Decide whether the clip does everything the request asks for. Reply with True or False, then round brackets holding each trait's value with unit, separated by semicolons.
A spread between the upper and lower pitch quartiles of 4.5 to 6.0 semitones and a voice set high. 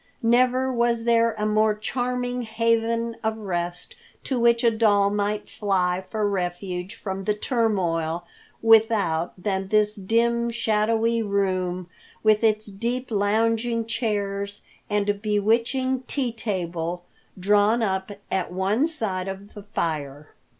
False (3.2 semitones; 210 Hz)